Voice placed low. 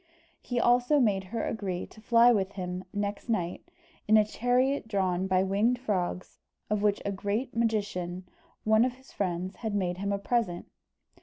No: high, 205 Hz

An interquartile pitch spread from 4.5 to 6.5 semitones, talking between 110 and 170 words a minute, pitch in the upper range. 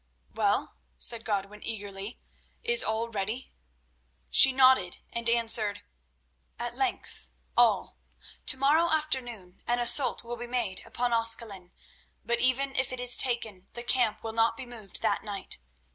No: average, 3.2 semitones; average, 145 wpm; high, 235 Hz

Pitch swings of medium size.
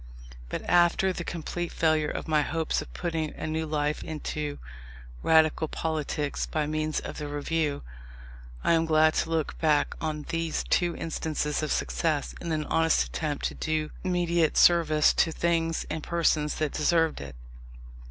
No: narrow, 1.4 semitones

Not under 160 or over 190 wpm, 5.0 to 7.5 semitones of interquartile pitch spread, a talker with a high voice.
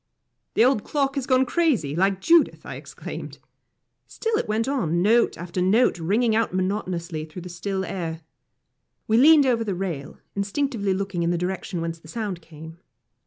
Yes: average, 170 wpm; wide, 5.6 semitones; high, 195 Hz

